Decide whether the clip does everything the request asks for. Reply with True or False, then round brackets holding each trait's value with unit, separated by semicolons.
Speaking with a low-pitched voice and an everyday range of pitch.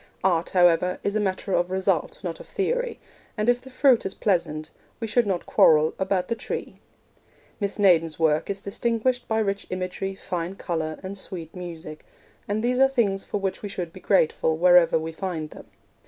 False (190 Hz; 3.8 semitones)